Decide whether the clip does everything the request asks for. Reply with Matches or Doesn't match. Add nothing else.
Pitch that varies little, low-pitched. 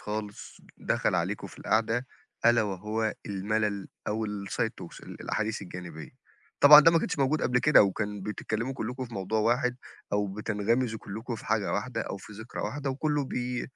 Doesn't match